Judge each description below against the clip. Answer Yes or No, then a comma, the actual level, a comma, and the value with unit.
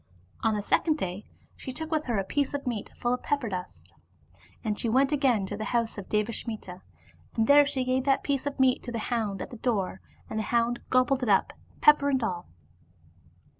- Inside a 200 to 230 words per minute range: Yes, fast, 205 wpm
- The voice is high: Yes, high, 240 Hz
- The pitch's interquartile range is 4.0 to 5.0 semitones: Yes, average, 4.3 semitones